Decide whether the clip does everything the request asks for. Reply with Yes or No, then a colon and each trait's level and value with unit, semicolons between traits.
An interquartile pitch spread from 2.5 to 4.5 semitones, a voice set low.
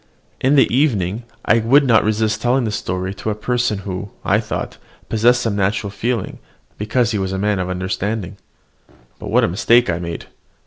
Yes: average, 3.9 semitones; low, 105 Hz